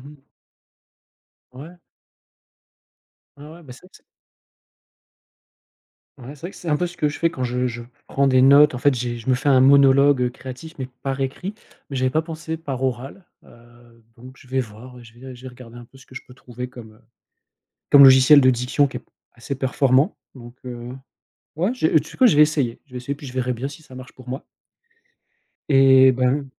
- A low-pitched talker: Yes, low, 130 Hz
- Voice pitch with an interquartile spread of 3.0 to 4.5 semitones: No, narrow, 2.5 semitones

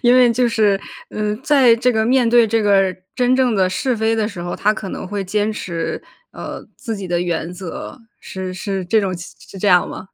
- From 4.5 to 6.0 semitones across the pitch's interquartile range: No, average, 3.8 semitones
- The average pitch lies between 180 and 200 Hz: No, high, 210 Hz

